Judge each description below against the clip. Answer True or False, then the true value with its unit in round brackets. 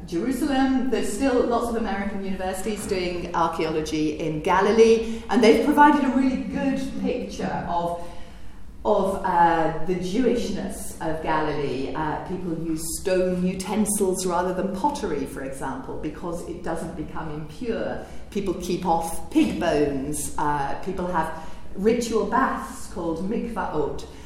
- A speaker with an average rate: False (130 wpm)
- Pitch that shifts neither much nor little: False (5.7 semitones)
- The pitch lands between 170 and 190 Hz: True (185 Hz)